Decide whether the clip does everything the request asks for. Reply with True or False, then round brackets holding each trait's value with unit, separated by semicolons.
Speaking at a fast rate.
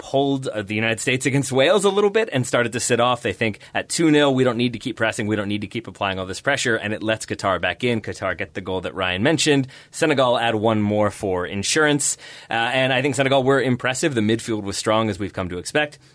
True (255 wpm)